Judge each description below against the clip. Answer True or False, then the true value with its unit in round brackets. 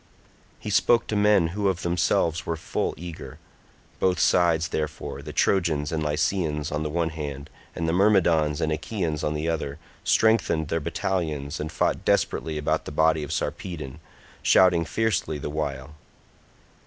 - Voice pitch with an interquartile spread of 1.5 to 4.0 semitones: True (2.7 semitones)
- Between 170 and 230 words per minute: False (155 wpm)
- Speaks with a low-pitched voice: True (80 Hz)